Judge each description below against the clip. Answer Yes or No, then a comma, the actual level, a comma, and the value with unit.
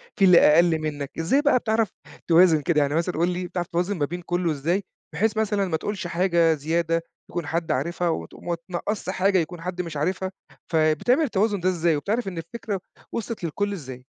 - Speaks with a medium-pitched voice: Yes, medium, 175 Hz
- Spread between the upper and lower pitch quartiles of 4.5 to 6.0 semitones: No, average, 3.1 semitones